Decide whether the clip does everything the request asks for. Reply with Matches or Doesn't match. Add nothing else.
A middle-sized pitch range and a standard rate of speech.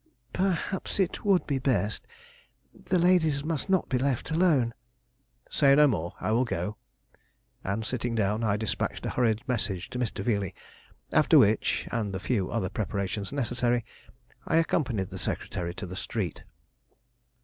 Doesn't match